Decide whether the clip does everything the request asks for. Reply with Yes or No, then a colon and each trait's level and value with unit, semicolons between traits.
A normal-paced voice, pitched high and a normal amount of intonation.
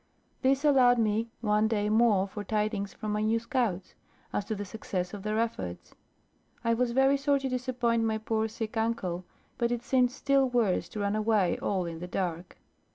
Yes: average, 190 wpm; high, 220 Hz; average, 3.0 semitones